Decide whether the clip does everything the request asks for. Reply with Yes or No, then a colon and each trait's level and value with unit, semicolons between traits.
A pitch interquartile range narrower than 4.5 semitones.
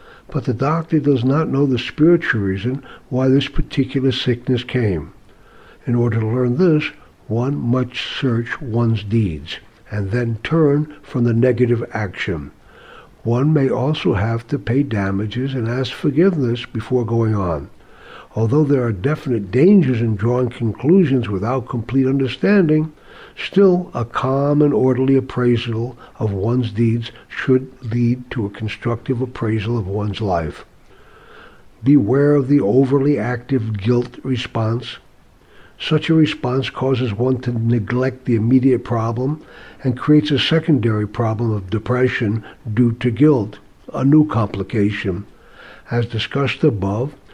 Yes: average, 3.2 semitones